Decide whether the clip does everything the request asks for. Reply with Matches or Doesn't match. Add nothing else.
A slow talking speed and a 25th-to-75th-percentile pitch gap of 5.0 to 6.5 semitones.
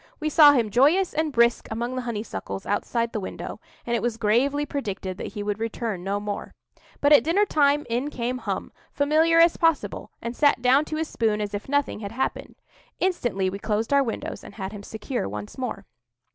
Doesn't match